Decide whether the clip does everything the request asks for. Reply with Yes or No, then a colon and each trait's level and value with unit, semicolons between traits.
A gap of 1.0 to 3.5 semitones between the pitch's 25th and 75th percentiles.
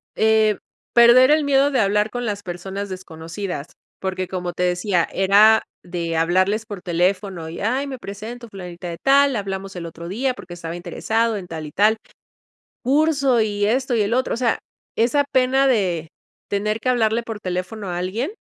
No: average, 4.8 semitones